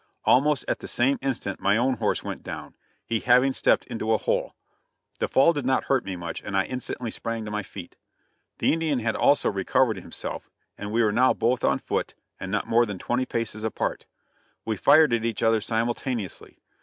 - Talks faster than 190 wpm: Yes, average, 200 wpm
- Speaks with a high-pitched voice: No, low, 115 Hz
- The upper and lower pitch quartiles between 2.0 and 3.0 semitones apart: No, average, 3.4 semitones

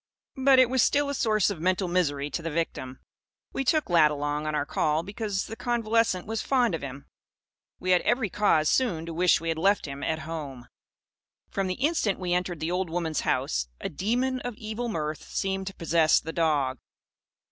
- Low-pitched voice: No, medium, 180 Hz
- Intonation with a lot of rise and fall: Yes, wide, 6.0 semitones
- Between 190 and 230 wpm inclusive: Yes, average, 200 wpm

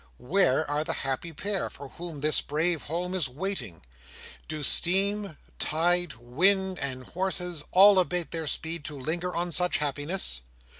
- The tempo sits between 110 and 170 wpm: Yes, average, 150 wpm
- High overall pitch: No, medium, 165 Hz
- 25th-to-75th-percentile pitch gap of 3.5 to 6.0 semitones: Yes, average, 4.0 semitones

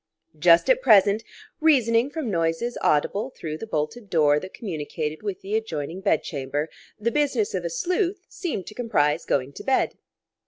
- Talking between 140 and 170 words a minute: Yes, average, 165 wpm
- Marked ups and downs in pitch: Yes, wide, 8.4 semitones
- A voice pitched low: No, high, 200 Hz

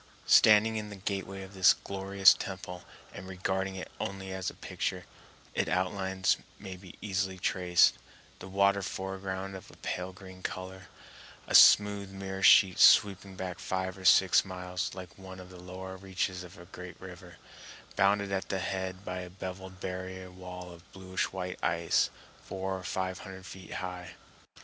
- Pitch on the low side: Yes, very low, 95 Hz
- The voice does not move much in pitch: Yes, narrow, 0.9 semitones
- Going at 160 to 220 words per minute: Yes, average, 165 wpm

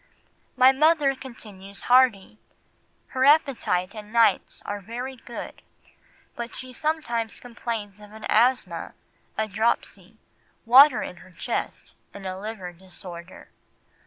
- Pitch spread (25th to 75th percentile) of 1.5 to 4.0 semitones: No, average, 4.4 semitones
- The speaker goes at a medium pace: No, slow, 120 wpm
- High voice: Yes, high, 225 Hz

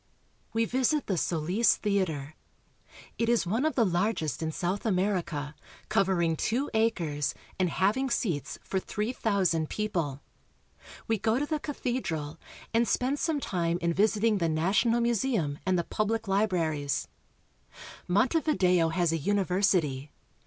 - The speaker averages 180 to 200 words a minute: No, average, 145 wpm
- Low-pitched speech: No, high, 190 Hz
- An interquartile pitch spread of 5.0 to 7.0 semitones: Yes, wide, 5.5 semitones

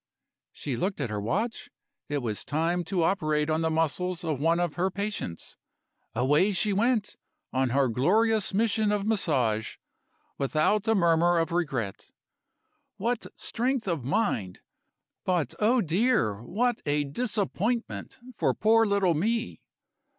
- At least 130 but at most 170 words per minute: Yes, slow, 135 wpm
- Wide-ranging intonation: Yes, wide, 6.4 semitones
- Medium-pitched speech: Yes, medium, 175 Hz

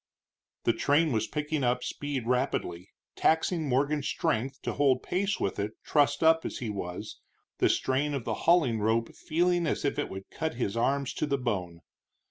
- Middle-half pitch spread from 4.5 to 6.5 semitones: Yes, average, 5.0 semitones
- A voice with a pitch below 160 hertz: Yes, low, 135 Hz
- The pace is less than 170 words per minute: No, average, 180 wpm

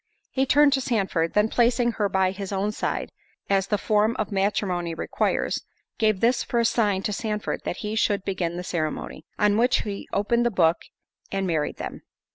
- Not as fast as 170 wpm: No, average, 180 wpm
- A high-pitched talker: Yes, high, 205 Hz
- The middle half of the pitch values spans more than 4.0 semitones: No, average, 3.2 semitones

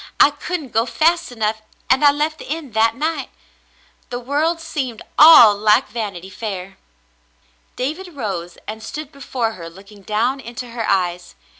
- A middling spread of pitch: No, wide, 5.7 semitones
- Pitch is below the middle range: No, high, 240 Hz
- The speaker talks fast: No, average, 155 wpm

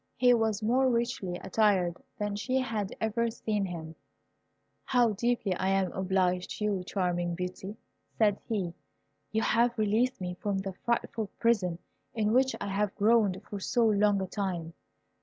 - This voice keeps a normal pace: Yes, average, 160 wpm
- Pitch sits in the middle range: No, high, 205 Hz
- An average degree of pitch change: Yes, average, 3.4 semitones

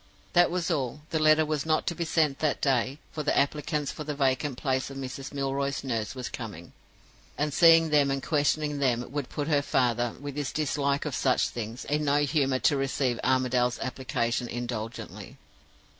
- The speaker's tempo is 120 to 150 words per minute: No, average, 185 wpm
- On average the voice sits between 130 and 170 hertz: Yes, medium, 140 Hz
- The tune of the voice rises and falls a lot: No, average, 2.8 semitones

